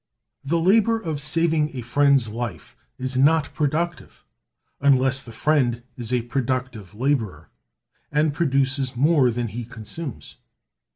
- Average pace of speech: No, slow, 125 wpm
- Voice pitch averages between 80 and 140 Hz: Yes, low, 135 Hz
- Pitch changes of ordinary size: Yes, average, 3.9 semitones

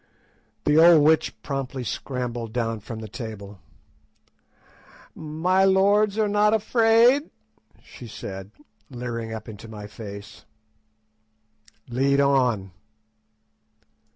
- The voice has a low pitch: Yes, low, 130 Hz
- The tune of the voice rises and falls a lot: Yes, wide, 8.7 semitones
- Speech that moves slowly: Yes, slow, 100 wpm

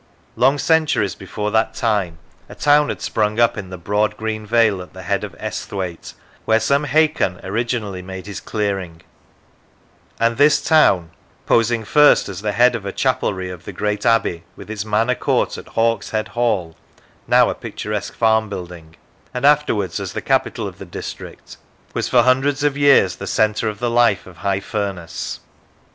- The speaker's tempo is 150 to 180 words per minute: Yes, average, 175 wpm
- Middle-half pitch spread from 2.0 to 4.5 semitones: Yes, average, 3.7 semitones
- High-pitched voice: No, low, 105 Hz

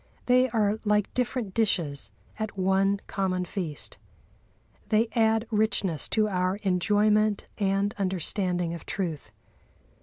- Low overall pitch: No, high, 200 Hz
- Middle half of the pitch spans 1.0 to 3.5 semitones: Yes, average, 2.9 semitones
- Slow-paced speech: Yes, slow, 115 wpm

